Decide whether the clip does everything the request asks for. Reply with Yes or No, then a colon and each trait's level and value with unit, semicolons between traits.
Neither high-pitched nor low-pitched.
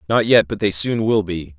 No: low, 100 Hz